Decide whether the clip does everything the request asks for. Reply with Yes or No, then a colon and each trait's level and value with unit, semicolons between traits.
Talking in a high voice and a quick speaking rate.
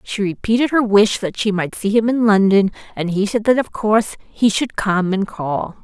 Yes: high, 210 Hz; fast, 225 wpm